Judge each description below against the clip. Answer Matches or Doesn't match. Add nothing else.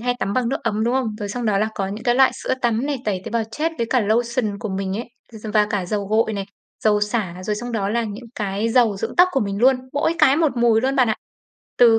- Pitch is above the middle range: Matches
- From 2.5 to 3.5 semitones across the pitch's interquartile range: Matches